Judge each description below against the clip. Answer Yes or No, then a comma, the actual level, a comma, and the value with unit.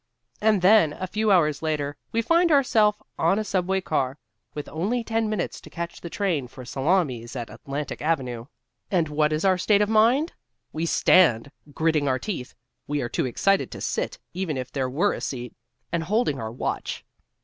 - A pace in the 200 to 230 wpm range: No, average, 185 wpm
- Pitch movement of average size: No, wide, 6.6 semitones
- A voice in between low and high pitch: Yes, medium, 165 Hz